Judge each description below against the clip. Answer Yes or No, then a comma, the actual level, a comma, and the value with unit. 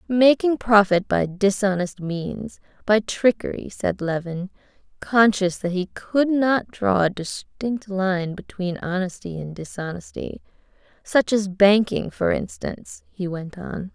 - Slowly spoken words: Yes, slow, 130 wpm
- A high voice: Yes, high, 200 Hz